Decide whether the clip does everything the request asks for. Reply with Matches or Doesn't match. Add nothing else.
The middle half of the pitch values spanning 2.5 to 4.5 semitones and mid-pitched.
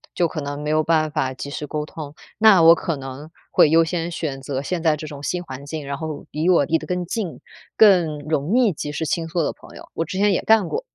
Matches